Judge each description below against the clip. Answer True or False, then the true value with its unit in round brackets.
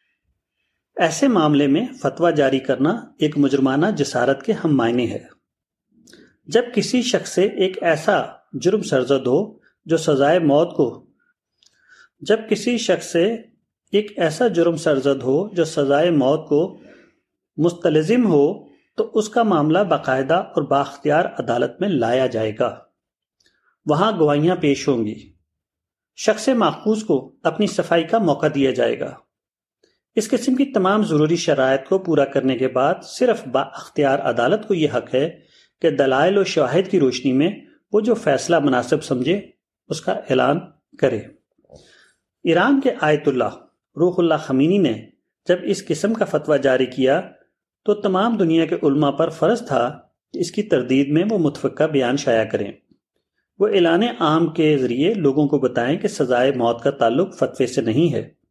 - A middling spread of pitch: False (6.9 semitones)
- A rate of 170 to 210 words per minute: False (155 wpm)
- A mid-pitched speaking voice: True (160 Hz)